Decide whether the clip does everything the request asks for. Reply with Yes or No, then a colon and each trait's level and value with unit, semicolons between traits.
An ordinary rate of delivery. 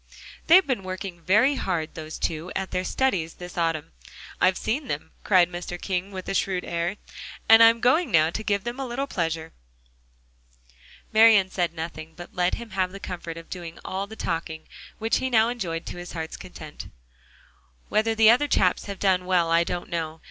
Yes: average, 190 wpm